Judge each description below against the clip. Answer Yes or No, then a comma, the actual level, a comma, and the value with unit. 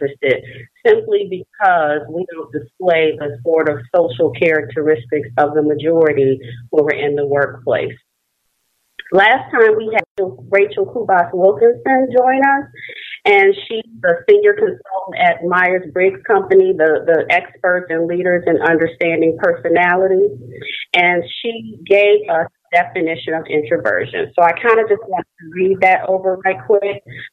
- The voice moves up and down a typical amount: No, wide, 5.9 semitones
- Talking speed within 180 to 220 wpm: No, average, 140 wpm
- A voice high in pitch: No, medium, 180 Hz